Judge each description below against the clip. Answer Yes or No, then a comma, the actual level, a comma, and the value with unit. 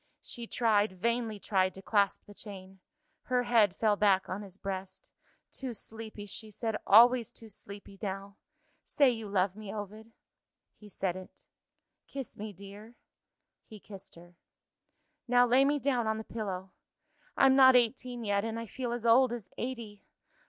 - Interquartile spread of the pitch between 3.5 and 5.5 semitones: No, average, 3.1 semitones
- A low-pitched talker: No, high, 215 Hz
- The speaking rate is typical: Yes, average, 160 wpm